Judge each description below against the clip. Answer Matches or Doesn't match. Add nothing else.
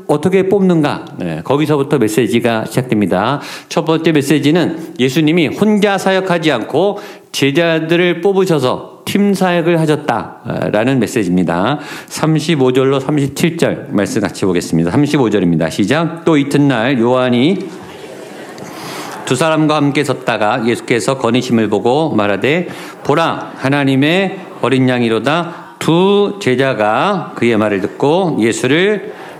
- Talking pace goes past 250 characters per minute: Matches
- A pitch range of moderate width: Doesn't match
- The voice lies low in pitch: Doesn't match